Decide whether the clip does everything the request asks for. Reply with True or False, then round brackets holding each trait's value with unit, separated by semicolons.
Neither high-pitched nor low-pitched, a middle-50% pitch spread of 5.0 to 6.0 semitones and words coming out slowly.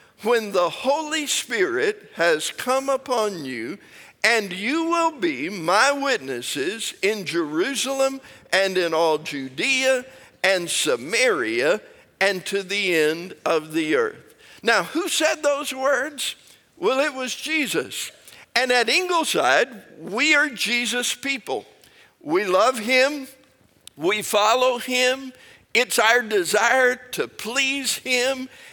False (260 Hz; 5.5 semitones; 120 wpm)